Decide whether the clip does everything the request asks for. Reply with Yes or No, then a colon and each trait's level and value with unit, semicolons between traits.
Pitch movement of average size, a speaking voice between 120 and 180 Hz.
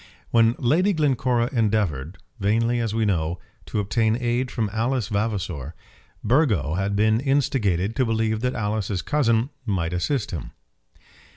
No: average, 3.6 semitones; low, 110 Hz